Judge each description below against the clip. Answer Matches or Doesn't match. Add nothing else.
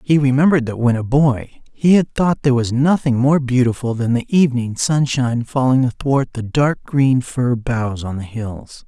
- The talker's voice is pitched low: Matches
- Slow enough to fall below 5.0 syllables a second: Matches